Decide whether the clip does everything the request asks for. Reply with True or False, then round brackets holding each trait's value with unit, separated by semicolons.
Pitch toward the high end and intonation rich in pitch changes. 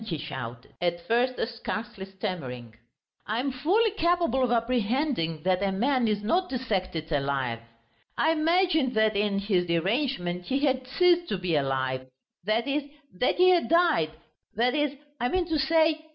True (230 Hz; 8.9 semitones)